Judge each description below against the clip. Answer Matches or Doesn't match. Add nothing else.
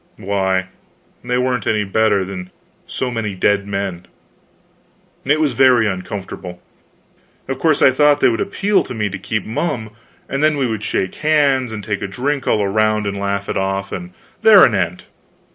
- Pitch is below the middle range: Matches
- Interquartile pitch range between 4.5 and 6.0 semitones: Matches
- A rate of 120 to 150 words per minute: Doesn't match